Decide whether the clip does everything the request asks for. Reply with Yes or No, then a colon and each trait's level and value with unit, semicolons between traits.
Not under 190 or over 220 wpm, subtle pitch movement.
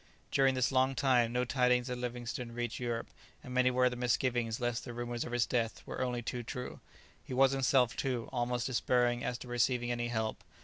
Yes: fast, 205 wpm; narrow, 0.9 semitones